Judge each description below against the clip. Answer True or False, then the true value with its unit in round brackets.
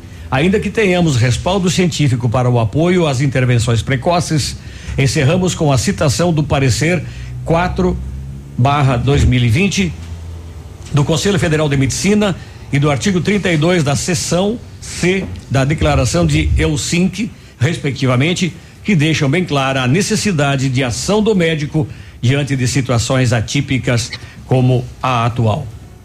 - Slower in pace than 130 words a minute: True (120 wpm)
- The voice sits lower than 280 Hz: True (140 Hz)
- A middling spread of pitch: False (5.8 semitones)